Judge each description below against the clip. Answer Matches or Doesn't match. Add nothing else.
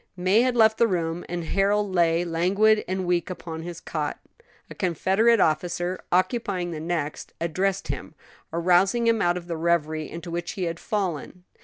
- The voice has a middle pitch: Matches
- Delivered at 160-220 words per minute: Matches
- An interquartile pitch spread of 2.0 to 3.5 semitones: Matches